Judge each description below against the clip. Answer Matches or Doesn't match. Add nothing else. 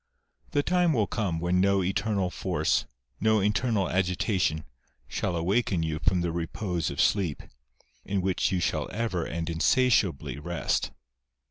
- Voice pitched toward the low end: Matches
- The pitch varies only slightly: Doesn't match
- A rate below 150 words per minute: Matches